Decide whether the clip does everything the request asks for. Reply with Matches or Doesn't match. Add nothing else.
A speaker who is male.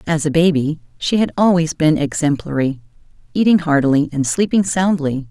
Doesn't match